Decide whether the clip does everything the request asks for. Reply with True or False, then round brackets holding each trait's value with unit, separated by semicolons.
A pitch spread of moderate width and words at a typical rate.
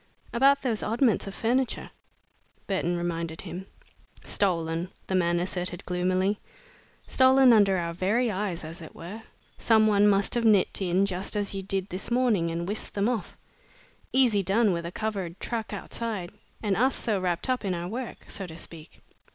True (4.1 semitones; 170 wpm)